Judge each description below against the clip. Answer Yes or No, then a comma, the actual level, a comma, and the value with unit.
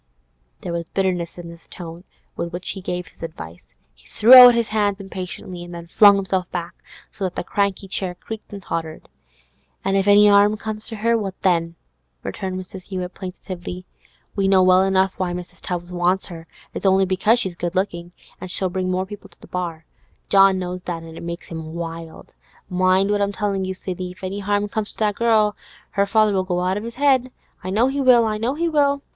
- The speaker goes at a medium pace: No, fast, 210 wpm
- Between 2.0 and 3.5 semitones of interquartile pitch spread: Yes, narrow, 2.6 semitones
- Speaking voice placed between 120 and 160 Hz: No, high, 190 Hz